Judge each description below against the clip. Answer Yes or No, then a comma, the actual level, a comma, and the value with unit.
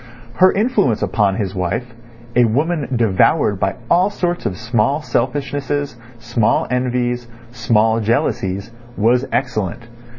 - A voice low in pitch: Yes, low, 120 Hz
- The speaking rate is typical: No, slow, 120 wpm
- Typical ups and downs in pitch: Yes, average, 4.4 semitones